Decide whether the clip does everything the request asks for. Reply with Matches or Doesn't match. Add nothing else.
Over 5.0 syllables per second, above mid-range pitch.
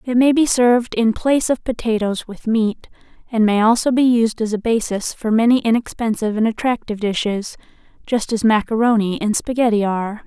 Matches